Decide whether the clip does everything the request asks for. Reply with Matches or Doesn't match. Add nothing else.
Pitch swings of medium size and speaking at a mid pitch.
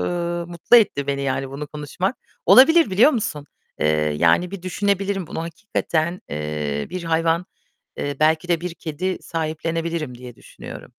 Matches